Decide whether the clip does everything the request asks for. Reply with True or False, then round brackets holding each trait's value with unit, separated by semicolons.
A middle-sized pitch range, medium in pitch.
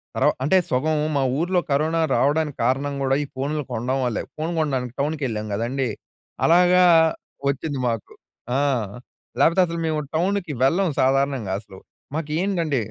True (3.8 semitones; 145 Hz)